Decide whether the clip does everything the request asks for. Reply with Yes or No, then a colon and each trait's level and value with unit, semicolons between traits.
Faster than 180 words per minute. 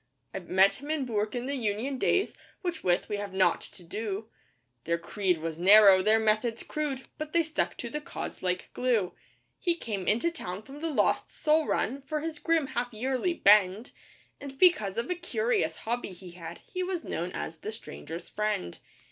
Yes: average, 190 wpm